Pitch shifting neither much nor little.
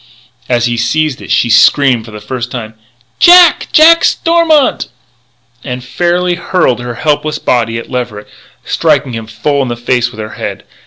Yes: average, 4.8 semitones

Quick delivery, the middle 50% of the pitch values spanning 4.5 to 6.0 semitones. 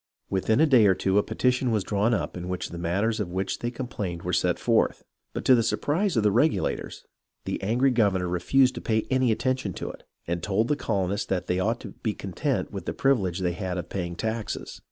Yes: fast, 230 wpm; average, 4.8 semitones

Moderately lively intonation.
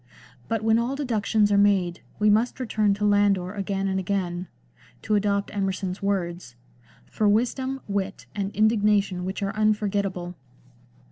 No: narrow, 2.0 semitones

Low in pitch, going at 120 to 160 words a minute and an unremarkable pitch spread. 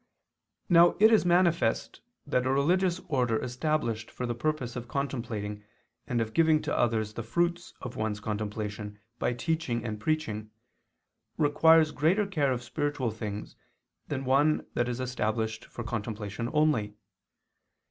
No: low, 125 Hz; average, 140 wpm; wide, 5.9 semitones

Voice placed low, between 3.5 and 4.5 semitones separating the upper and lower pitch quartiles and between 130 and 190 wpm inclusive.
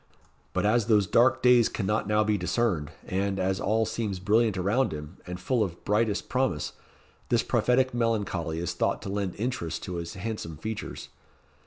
Yes: low, 105 Hz; average, 4.1 semitones; average, 170 wpm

